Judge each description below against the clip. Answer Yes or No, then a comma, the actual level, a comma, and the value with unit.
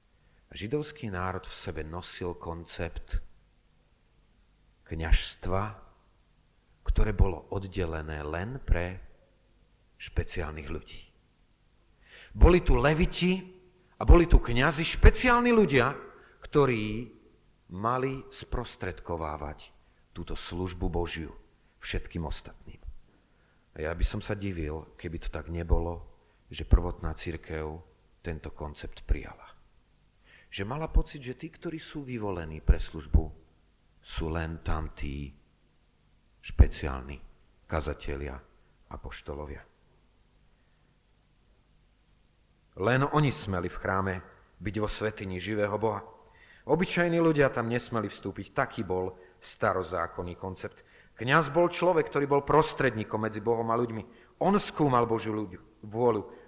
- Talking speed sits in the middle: No, slow, 105 wpm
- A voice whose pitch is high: No, very low, 95 Hz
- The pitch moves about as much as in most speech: No, wide, 6.7 semitones